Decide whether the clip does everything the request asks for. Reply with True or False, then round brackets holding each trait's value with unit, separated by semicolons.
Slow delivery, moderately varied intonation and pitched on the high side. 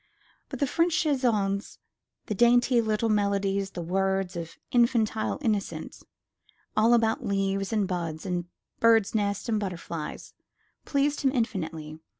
True (130 wpm; 3.5 semitones; 205 Hz)